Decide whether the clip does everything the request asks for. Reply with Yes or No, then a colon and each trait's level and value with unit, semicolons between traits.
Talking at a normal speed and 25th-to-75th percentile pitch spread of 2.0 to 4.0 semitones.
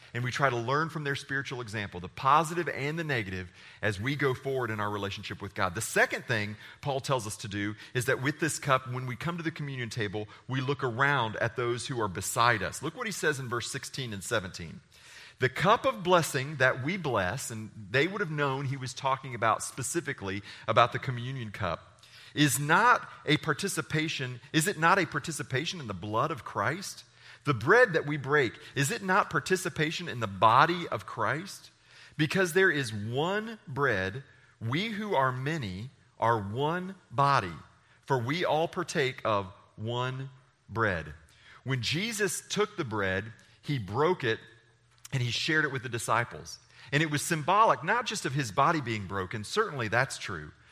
No: average, 185 wpm; average, 5.1 semitones